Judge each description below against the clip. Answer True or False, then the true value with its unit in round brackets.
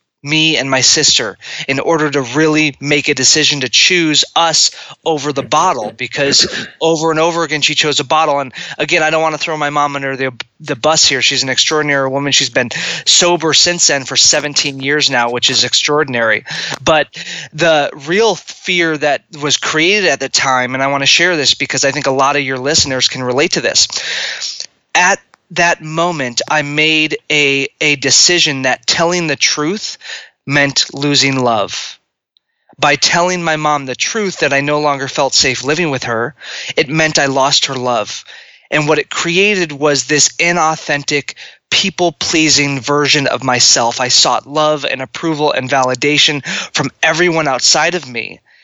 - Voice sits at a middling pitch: True (145 Hz)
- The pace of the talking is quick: False (180 wpm)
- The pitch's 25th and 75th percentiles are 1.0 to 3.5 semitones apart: True (2.6 semitones)